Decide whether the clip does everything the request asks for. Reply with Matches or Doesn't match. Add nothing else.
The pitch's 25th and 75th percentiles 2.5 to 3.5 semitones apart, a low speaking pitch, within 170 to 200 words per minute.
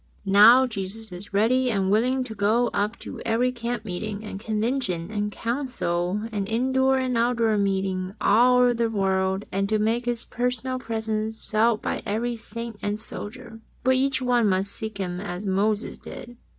Doesn't match